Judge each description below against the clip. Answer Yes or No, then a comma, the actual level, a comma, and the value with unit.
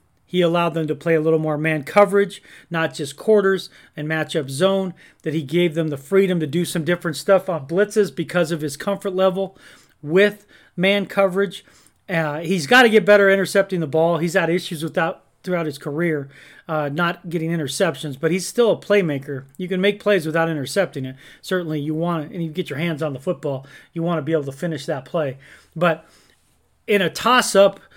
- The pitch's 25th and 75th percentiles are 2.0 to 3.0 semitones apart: No, average, 3.6 semitones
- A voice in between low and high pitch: Yes, medium, 170 Hz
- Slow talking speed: No, average, 200 wpm